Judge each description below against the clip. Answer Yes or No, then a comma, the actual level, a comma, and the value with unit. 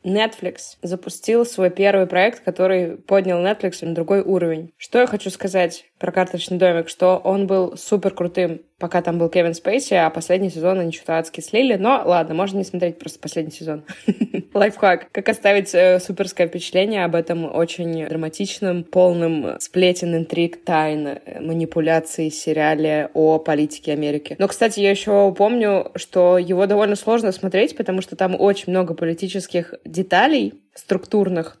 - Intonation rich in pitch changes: No, average, 2.8 semitones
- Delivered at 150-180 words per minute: Yes, average, 155 wpm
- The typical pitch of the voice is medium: Yes, medium, 180 Hz